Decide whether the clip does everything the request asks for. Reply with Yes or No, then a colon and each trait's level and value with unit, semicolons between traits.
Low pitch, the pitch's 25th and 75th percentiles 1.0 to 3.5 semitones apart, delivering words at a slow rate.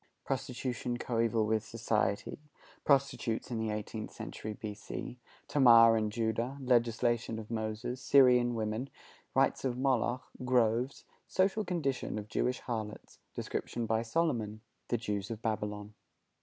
Yes: low, 115 Hz; narrow, 2.6 semitones; slow, 125 wpm